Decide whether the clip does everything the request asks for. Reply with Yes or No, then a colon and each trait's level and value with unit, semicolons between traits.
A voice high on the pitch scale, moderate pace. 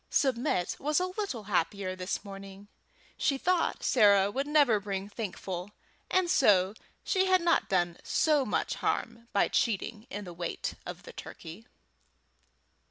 Yes: high, 210 Hz; average, 145 wpm